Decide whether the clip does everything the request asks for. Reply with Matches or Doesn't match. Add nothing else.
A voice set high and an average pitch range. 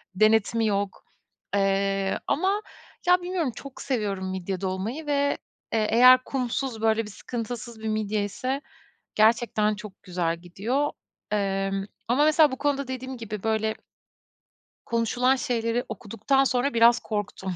Matches